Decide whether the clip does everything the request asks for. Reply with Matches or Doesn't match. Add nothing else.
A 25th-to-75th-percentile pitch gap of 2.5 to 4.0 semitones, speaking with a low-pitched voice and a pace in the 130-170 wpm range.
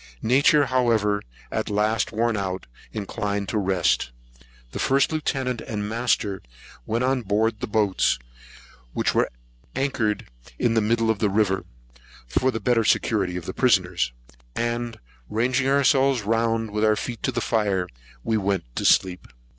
Matches